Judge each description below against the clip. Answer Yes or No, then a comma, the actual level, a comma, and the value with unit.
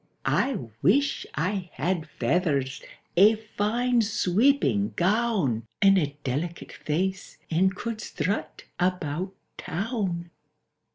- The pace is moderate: No, slow, 100 wpm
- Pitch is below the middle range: No, medium, 185 Hz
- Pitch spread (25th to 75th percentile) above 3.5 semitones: Yes, wide, 5.4 semitones